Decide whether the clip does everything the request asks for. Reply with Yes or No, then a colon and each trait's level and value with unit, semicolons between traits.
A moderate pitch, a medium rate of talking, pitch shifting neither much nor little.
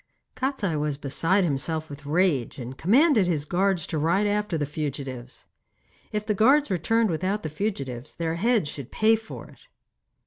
No: medium, 170 Hz; average, 165 wpm; wide, 6.2 semitones